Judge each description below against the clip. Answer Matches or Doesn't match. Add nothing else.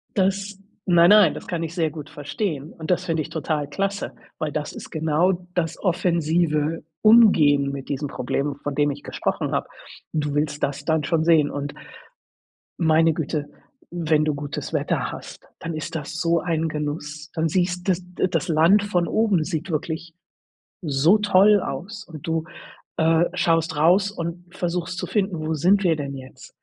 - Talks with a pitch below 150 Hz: Doesn't match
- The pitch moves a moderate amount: Matches